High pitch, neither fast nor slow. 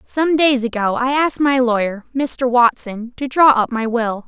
Yes: very high, 250 Hz; average, 195 wpm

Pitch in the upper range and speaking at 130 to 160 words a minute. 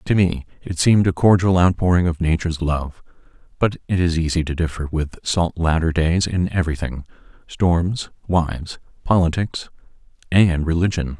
No: very low, 85 Hz; average, 140 wpm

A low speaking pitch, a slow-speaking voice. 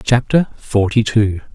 Yes: low, 110 Hz; slow, 115 wpm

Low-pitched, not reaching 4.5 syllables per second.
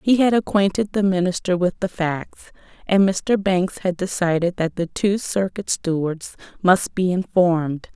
No: medium, 185 Hz; 4.3 syllables/s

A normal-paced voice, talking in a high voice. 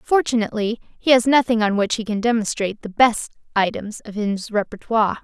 Yes: average, 170 wpm; high, 220 Hz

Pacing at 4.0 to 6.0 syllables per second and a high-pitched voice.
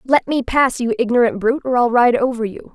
Yes: 5.9 syllables/s; very high, 250 Hz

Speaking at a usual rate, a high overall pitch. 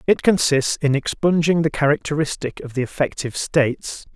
No: average, 145 wpm; medium, 145 Hz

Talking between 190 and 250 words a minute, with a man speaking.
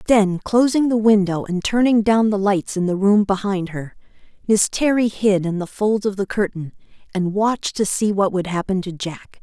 No: fast, 205 wpm; female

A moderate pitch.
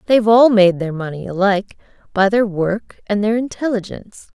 No: high, 205 Hz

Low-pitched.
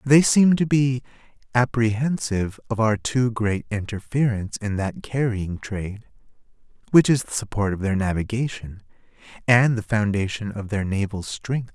Yes: low, 115 Hz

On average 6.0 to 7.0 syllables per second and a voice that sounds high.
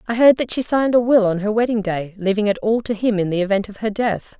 Yes: 6.2 syllables/s; high, 215 Hz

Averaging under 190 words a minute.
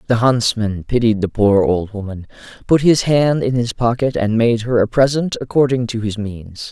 No: average, 195 wpm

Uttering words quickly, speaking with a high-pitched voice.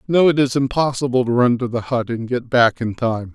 No: fast, 250 wpm; low, 125 Hz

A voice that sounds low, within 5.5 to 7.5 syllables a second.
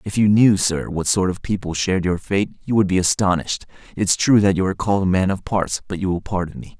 Yes: very low, 95 Hz; 6.0 syllables/s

